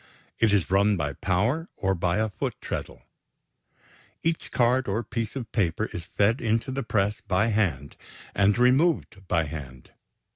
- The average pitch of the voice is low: Yes, low, 105 Hz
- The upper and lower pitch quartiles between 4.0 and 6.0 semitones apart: Yes, average, 4.4 semitones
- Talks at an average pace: Yes, average, 155 wpm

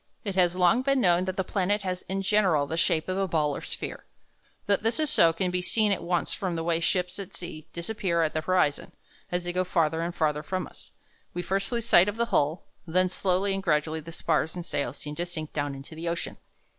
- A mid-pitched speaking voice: Yes, medium, 175 Hz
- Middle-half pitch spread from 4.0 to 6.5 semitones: No, average, 2.9 semitones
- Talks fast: Yes, fast, 245 wpm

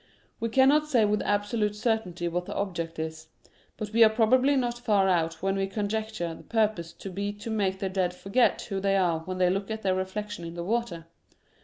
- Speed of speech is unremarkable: No, fast, 215 wpm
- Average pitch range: Yes, average, 3.5 semitones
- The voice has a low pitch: No, high, 200 Hz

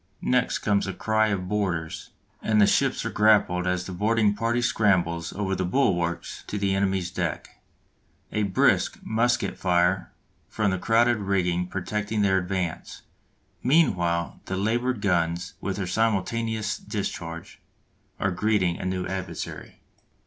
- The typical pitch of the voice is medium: No, very low, 95 Hz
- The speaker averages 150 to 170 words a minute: No, average, 140 wpm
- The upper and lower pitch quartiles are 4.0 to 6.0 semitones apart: No, average, 3.3 semitones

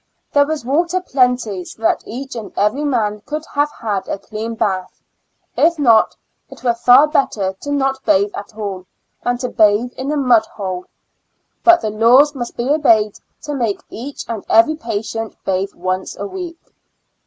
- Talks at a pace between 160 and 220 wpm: Yes, average, 175 wpm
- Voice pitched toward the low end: No, high, 235 Hz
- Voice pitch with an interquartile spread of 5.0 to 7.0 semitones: Yes, wide, 5.4 semitones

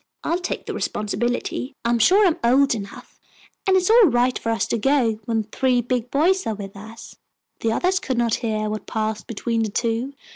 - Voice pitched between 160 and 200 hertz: No, high, 235 Hz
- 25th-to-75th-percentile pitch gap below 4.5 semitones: Yes, average, 4.0 semitones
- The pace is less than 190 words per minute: No, fast, 205 wpm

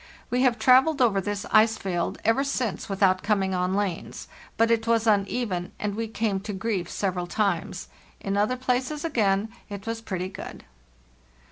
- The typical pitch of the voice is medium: No, high, 210 Hz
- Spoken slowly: No, average, 165 wpm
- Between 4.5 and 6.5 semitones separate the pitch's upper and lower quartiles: No, average, 3.1 semitones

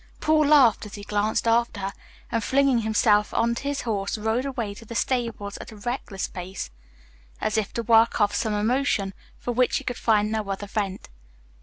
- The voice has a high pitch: Yes, high, 220 Hz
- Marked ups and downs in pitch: No, average, 2.7 semitones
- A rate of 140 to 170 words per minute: No, average, 190 wpm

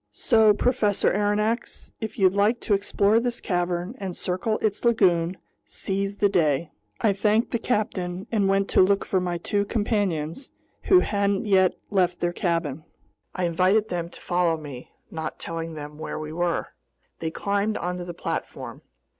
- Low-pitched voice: No, high, 190 Hz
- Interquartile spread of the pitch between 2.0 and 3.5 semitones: Yes, average, 3.2 semitones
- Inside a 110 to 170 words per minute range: Yes, average, 165 wpm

